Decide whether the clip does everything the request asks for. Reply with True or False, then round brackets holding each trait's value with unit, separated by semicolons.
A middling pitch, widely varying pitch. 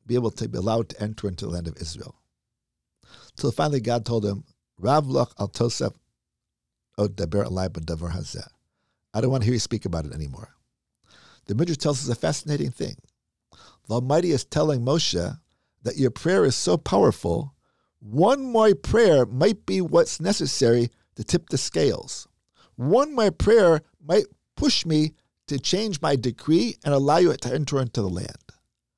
False (125 Hz; 7.4 semitones)